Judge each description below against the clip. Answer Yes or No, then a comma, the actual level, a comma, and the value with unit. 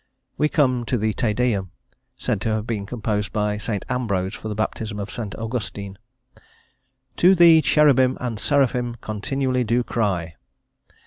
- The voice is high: No, low, 115 Hz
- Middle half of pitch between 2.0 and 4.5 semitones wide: Yes, average, 3.4 semitones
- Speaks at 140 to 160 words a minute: Yes, average, 150 wpm